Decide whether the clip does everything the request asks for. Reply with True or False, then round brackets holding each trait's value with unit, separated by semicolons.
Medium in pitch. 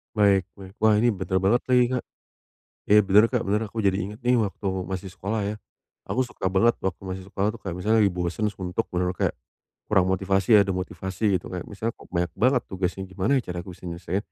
False (95 Hz)